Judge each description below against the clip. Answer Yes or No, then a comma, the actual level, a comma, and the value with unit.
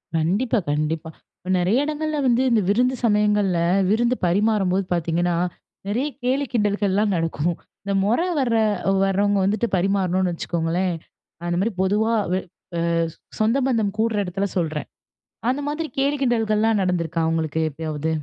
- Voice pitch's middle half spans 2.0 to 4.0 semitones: No, average, 4.8 semitones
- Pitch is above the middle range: Yes, high, 200 Hz